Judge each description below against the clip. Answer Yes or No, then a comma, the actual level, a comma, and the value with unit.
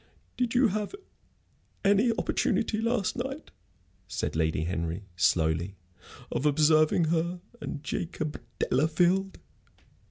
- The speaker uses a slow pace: Yes, slow, 100 wpm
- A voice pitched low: No, medium, 160 Hz